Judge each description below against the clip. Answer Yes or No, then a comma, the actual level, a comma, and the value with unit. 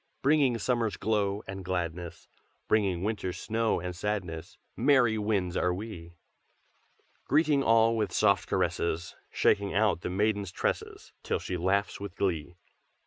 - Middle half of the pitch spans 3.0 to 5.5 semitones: Yes, average, 3.7 semitones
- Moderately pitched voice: No, low, 100 Hz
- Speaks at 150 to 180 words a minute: No, slow, 135 wpm